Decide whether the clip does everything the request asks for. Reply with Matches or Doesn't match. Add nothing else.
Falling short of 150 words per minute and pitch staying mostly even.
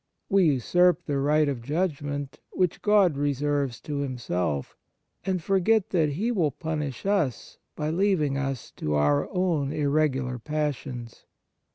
Doesn't match